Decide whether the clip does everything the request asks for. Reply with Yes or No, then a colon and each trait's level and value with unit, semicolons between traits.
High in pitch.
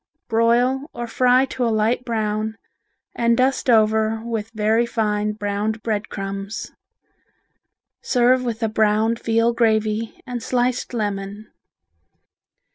Yes: high, 225 Hz